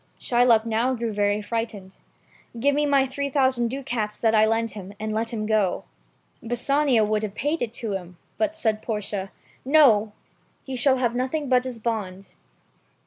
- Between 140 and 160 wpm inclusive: No, average, 180 wpm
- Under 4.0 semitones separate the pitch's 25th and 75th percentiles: Yes, average, 3.5 semitones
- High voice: Yes, high, 230 Hz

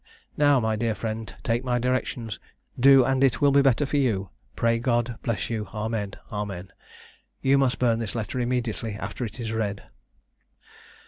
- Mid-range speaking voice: No, low, 115 Hz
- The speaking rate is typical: Yes, average, 170 wpm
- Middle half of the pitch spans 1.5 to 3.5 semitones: Yes, average, 2.8 semitones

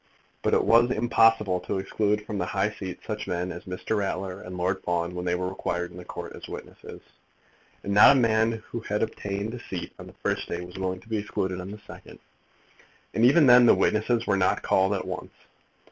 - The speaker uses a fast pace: Yes, fast, 220 wpm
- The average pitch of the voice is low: Yes, low, 100 Hz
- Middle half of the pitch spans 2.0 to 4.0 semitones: Yes, average, 3.4 semitones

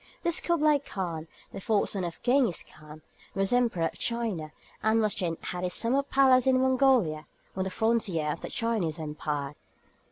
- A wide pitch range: Yes, wide, 7.3 semitones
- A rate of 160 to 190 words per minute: Yes, average, 170 wpm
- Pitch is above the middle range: Yes, high, 205 Hz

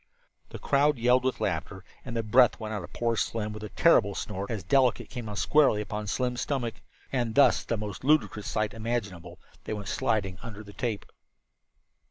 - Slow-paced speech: No, average, 190 wpm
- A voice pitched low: Yes, low, 110 Hz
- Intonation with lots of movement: No, average, 3.2 semitones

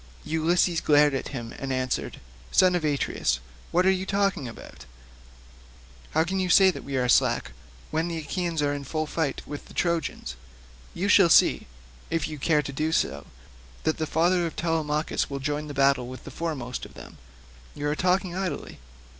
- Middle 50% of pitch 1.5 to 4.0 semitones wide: Yes, average, 3.7 semitones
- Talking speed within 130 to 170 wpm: No, average, 180 wpm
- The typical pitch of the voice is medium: Yes, medium, 155 Hz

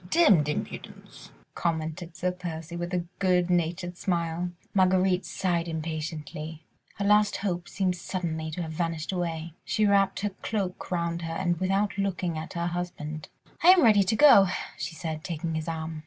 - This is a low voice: No, medium, 175 Hz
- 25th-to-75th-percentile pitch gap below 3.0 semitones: Yes, narrow, 2.6 semitones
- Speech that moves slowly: No, average, 165 wpm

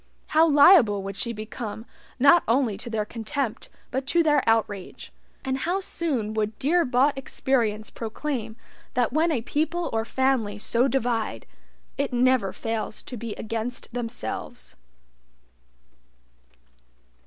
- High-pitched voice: Yes, high, 240 Hz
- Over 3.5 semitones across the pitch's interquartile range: Yes, average, 4.1 semitones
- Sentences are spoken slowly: Yes, slow, 130 wpm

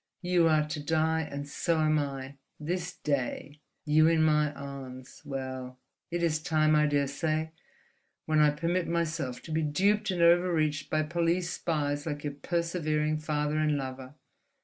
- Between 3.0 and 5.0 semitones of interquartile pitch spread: No, narrow, 2.4 semitones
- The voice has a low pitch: No, medium, 155 Hz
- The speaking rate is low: No, average, 150 wpm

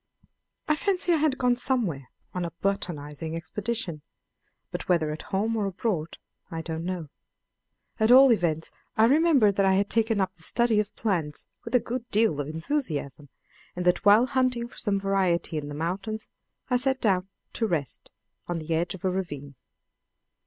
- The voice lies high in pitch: Yes, high, 195 Hz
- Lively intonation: Yes, wide, 6.1 semitones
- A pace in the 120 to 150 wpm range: No, average, 175 wpm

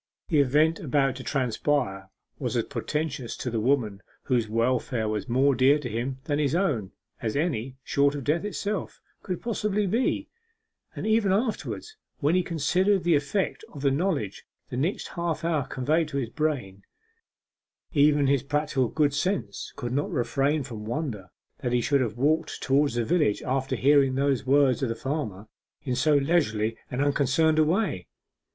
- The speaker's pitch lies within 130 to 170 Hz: Yes, medium, 140 Hz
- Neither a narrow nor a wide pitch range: Yes, average, 4.1 semitones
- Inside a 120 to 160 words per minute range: No, average, 170 wpm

